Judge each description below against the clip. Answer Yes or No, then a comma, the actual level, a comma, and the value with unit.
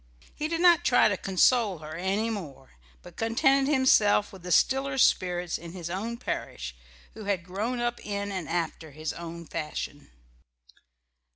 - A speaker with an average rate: Yes, average, 160 wpm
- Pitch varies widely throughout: Yes, wide, 5.9 semitones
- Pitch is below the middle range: No, high, 195 Hz